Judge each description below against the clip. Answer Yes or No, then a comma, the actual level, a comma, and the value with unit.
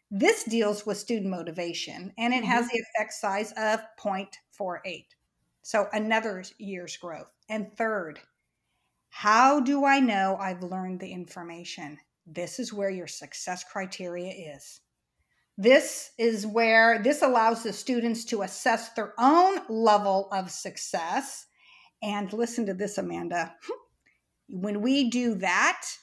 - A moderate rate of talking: No, slow, 130 wpm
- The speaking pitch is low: No, high, 210 Hz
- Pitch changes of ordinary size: Yes, average, 3.7 semitones